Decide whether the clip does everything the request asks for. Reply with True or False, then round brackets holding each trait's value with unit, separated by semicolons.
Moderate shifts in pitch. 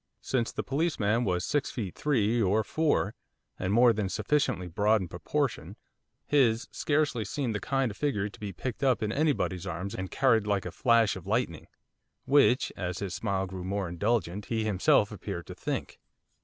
True (4.7 semitones)